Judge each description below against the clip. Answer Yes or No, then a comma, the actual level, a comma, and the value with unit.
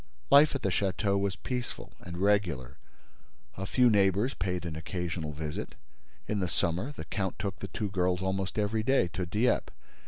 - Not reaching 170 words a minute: No, average, 175 wpm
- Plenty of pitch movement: No, average, 3.2 semitones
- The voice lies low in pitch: Yes, very low, 95 Hz